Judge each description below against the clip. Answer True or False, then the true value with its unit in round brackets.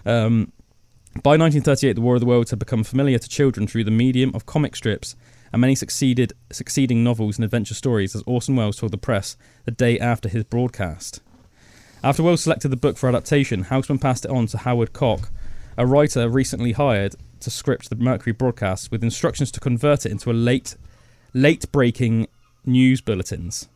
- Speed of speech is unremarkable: True (180 wpm)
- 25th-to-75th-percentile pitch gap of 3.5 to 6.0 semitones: False (2.7 semitones)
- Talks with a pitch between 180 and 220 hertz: False (120 Hz)